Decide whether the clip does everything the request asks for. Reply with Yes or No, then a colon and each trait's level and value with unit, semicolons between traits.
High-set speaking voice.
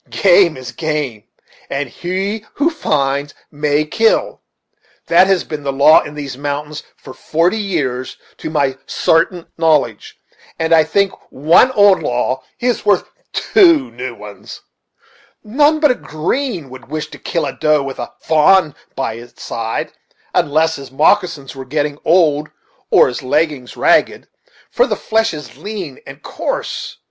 No: medium, 155 Hz